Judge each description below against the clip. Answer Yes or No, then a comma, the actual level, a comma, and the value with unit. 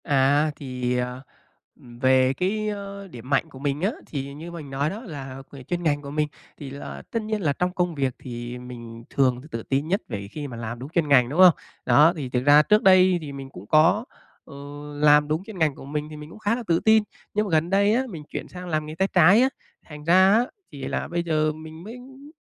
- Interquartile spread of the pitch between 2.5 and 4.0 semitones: No, average, 5.3 semitones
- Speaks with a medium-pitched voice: Yes, medium, 150 Hz